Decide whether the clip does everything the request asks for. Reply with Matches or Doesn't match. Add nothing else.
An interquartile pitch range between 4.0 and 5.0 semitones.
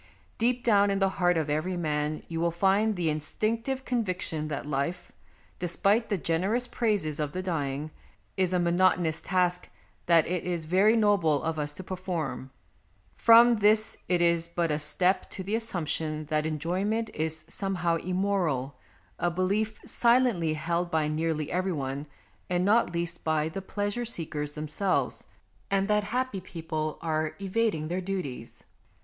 Matches